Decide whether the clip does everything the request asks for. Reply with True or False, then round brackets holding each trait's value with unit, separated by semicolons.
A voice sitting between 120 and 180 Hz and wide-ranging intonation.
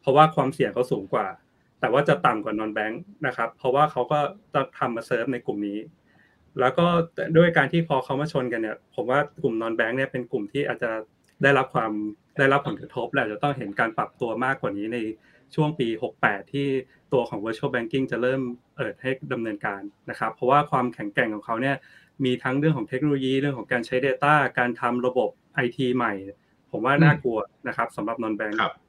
False (130 Hz; 3.9 semitones)